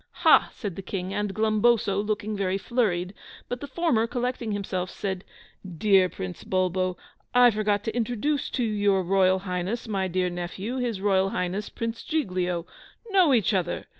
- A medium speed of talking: Yes, average, 160 wpm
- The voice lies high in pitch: Yes, high, 205 Hz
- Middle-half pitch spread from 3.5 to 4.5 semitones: Yes, average, 3.8 semitones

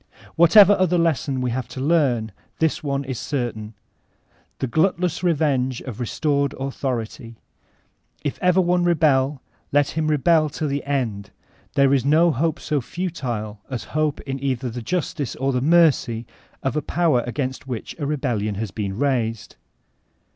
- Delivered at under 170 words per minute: Yes, average, 155 wpm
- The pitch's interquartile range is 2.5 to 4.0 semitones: No, average, 4.4 semitones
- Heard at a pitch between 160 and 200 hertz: No, medium, 140 Hz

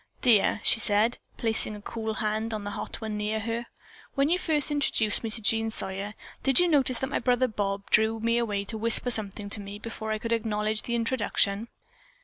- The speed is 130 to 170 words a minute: No, fast, 205 wpm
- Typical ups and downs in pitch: No, narrow, 2.1 semitones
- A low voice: No, high, 220 Hz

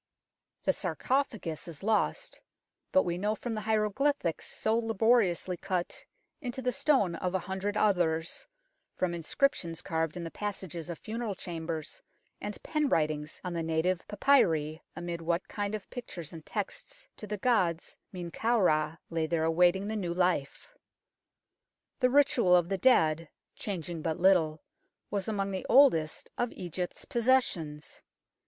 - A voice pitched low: No, medium, 185 Hz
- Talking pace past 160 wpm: No, average, 150 wpm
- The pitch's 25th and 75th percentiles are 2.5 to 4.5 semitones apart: No, average, 5.0 semitones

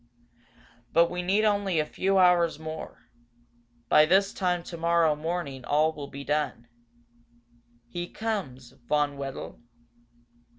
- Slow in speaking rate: Yes, slow, 120 wpm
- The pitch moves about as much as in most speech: Yes, average, 3.4 semitones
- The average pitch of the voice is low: No, medium, 165 Hz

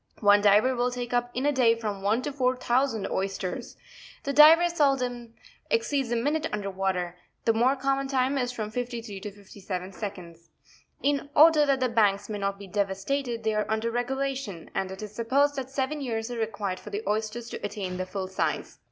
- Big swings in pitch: No, average, 4.8 semitones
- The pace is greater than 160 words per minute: Yes, average, 200 wpm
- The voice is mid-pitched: No, high, 230 Hz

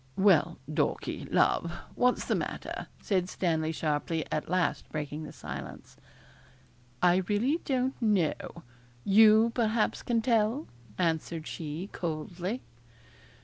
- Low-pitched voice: No, medium, 180 Hz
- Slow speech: Yes, slow, 110 wpm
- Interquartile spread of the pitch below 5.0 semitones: No, wide, 5.6 semitones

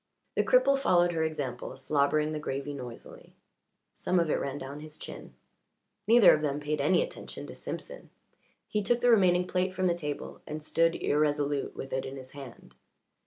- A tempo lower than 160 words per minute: No, average, 180 wpm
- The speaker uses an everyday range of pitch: Yes, average, 4.2 semitones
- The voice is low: No, medium, 155 Hz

